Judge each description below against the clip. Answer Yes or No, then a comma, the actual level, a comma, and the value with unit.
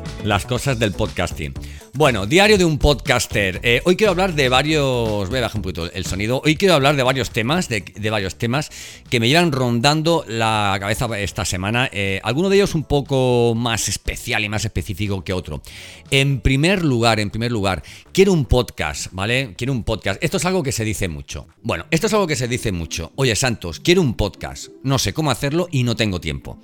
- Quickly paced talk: Yes, fast, 210 wpm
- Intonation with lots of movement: Yes, wide, 6.0 semitones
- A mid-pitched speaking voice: No, low, 120 Hz